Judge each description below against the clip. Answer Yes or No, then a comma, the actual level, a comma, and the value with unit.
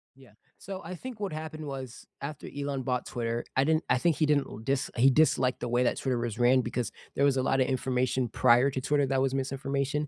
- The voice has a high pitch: No, low, 135 Hz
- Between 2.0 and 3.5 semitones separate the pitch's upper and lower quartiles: Yes, narrow, 2.6 semitones